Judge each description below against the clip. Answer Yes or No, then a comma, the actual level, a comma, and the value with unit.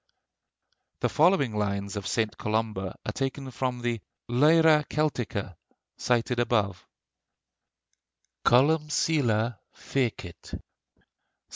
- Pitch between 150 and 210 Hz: No, low, 120 Hz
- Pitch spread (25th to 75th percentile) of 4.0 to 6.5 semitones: Yes, average, 4.9 semitones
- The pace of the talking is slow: Yes, slow, 90 wpm